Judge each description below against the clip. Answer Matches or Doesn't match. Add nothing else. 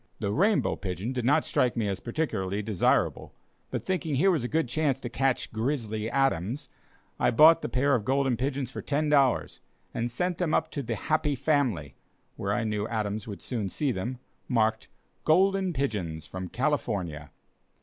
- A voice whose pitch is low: Matches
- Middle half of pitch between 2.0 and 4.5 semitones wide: Doesn't match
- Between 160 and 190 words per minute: Matches